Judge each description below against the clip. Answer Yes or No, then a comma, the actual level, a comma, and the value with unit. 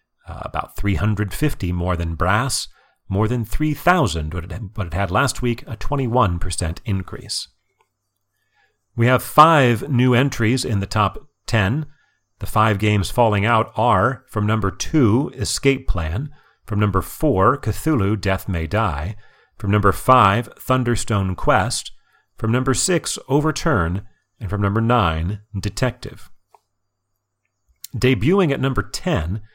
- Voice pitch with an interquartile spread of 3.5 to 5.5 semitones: Yes, average, 4.4 semitones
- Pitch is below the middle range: Yes, low, 105 Hz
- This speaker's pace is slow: Yes, slow, 125 wpm